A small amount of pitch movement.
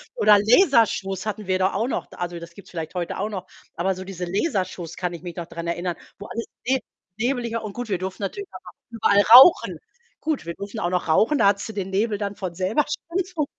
No: average, 4.4 semitones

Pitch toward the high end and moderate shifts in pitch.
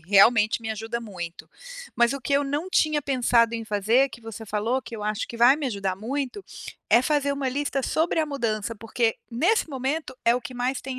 Yes: high, 245 Hz; average, 3.8 semitones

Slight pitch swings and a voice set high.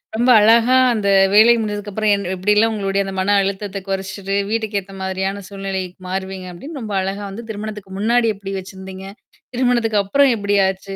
Yes: narrow, 2.1 semitones; high, 200 Hz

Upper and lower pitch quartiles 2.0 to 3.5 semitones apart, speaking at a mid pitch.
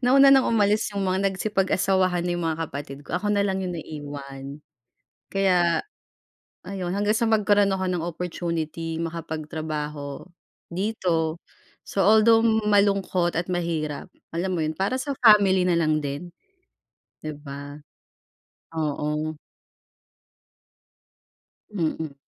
No: average, 4.2 semitones; medium, 175 Hz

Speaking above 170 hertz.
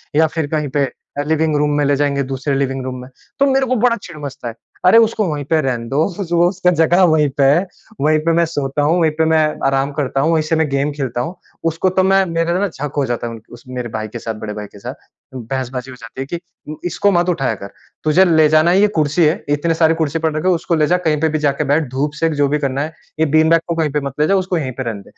No: medium, 150 Hz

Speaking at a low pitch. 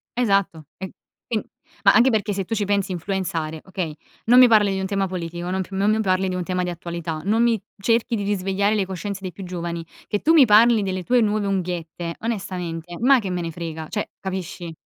No: high, 190 Hz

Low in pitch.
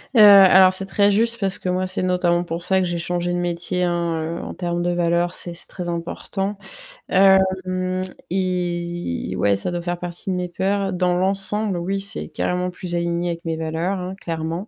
No: medium, 180 Hz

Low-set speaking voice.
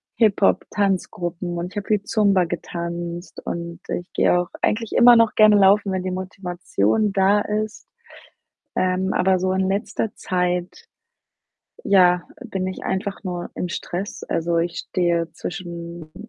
No: medium, 185 Hz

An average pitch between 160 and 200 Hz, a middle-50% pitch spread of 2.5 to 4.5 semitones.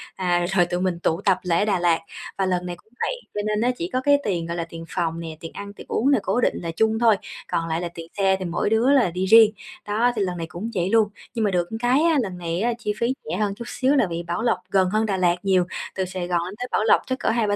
Yes: high, 190 Hz; average, 4.2 semitones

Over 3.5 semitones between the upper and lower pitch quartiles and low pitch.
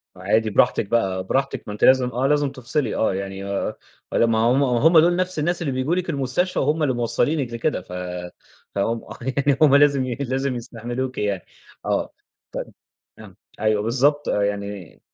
Yes: average, 4.6 semitones; low, 130 Hz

